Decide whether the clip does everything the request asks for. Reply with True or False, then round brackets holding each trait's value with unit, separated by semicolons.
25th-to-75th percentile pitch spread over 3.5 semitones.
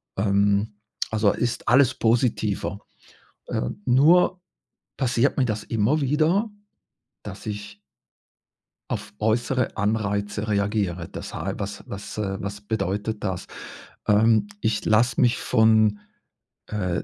False (2.8 semitones)